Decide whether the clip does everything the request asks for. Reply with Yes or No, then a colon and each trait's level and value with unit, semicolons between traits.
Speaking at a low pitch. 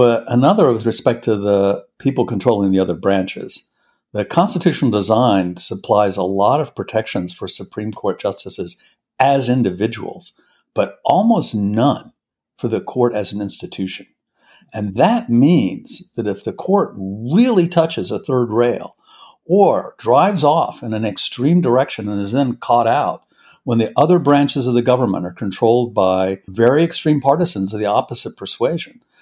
Yes: low, 120 Hz